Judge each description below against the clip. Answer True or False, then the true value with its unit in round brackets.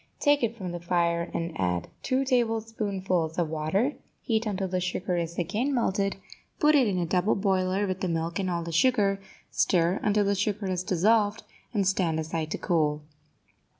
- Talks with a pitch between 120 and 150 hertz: False (190 Hz)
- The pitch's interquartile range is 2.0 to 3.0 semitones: False (3.8 semitones)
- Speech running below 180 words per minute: False (185 wpm)